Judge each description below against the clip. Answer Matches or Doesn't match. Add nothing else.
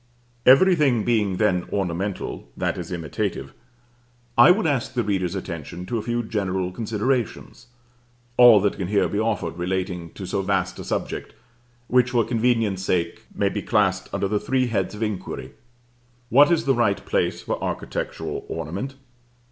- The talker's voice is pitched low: Matches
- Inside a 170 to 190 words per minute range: Doesn't match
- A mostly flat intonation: Doesn't match